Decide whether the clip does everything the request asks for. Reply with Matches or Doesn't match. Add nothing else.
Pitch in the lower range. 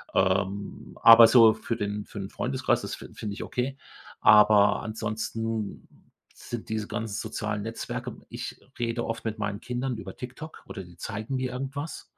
Matches